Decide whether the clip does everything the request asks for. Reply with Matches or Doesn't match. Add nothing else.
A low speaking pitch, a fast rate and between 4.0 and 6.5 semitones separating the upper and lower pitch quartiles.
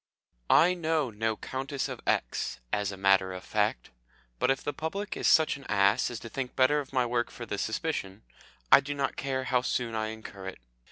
Matches